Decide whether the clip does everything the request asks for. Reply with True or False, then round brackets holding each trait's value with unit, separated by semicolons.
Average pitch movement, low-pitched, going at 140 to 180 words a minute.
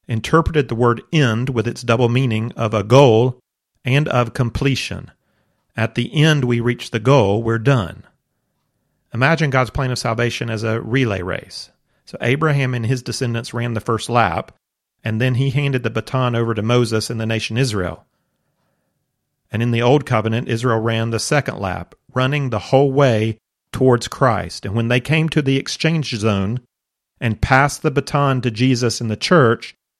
True (3.0 semitones; 120 Hz; 175 wpm)